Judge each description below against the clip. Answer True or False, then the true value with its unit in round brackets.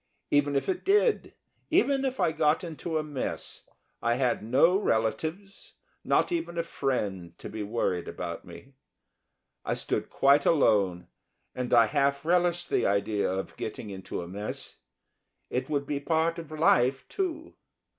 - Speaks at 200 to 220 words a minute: False (155 wpm)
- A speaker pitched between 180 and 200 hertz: False (140 Hz)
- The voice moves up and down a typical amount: False (7.2 semitones)